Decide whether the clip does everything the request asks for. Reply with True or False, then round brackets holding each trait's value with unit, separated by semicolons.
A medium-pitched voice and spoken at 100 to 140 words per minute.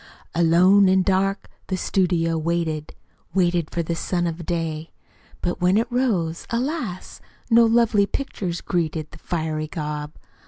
True (175 Hz; 135 wpm)